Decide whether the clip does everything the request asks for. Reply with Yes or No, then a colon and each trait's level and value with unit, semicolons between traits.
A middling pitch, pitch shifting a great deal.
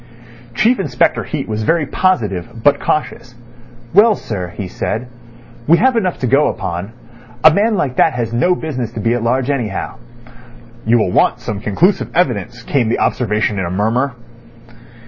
No: low, 120 Hz; wide, 6.6 semitones